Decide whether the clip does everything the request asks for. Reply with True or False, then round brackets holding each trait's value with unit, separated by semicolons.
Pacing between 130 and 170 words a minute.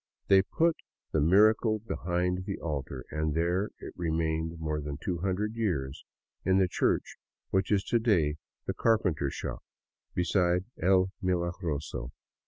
True (140 wpm)